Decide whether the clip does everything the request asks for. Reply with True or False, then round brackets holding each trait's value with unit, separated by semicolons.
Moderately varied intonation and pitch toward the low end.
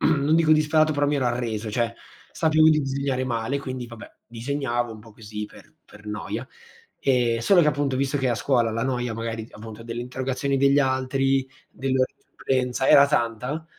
True (3.3 semitones; 130 Hz)